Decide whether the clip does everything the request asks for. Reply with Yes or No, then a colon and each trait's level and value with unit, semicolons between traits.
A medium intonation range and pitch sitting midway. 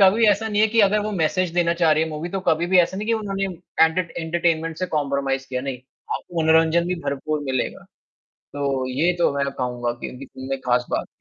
Yes: average, 4.9 semitones; medium, 160 Hz